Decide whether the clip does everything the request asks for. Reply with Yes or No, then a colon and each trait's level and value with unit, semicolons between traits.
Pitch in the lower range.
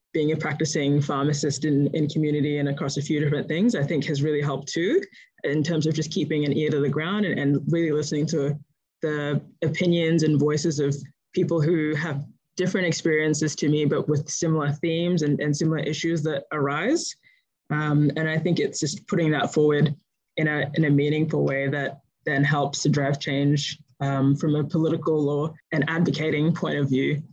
No: medium, 150 Hz